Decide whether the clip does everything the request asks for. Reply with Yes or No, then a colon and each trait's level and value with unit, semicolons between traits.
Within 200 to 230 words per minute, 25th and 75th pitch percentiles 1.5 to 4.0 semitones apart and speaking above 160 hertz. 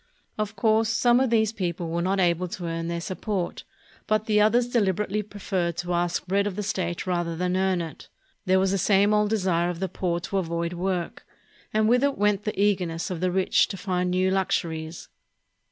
Yes: fast, 205 wpm; average, 3.1 semitones; high, 190 Hz